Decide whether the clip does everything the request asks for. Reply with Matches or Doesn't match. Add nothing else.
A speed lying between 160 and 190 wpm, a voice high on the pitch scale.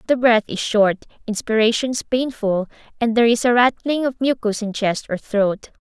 Matches